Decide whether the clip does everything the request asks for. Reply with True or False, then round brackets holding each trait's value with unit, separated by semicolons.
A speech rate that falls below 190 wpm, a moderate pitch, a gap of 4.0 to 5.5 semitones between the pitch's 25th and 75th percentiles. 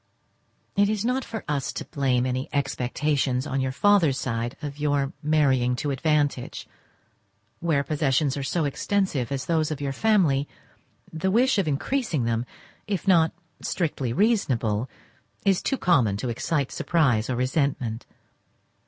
True (145 wpm; 145 Hz; 4.7 semitones)